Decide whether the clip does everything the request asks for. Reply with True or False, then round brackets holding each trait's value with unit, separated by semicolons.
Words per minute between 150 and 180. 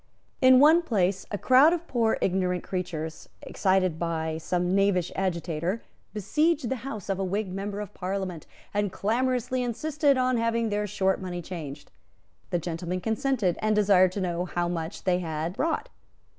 True (160 wpm)